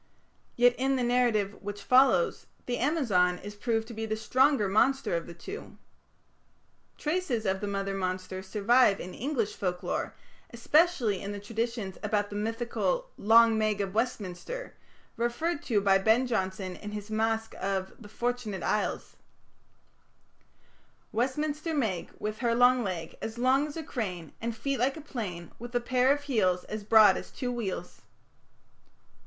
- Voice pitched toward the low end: No, high, 225 Hz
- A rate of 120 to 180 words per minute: Yes, average, 155 wpm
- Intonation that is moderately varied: Yes, average, 4.1 semitones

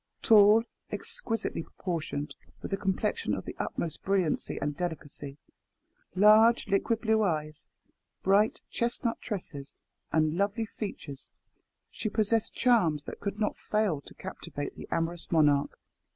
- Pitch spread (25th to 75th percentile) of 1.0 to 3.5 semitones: No, wide, 5.6 semitones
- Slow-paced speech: Yes, slow, 125 wpm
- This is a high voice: Yes, high, 195 Hz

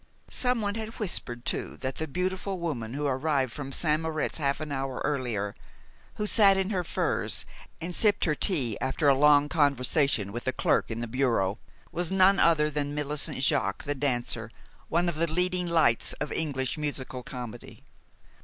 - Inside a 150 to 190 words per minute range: Yes, average, 170 wpm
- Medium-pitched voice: Yes, medium, 145 Hz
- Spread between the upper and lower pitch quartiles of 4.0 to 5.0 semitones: Yes, average, 4.7 semitones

